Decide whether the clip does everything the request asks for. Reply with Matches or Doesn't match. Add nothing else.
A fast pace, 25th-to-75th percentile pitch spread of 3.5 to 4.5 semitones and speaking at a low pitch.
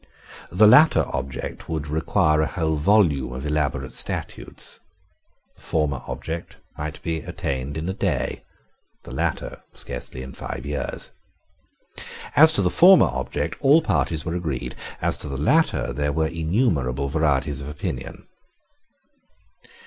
Doesn't match